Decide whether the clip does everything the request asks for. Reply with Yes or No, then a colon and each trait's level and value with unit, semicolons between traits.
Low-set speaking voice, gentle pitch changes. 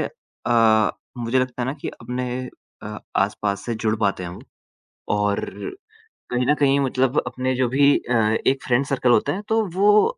No: low, 125 Hz; average, 3.5 semitones